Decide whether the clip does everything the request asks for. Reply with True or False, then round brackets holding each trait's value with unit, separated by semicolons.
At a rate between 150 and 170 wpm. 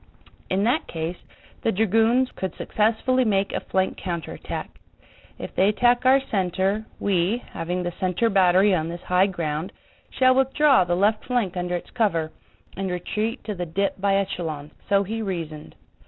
True (160 wpm)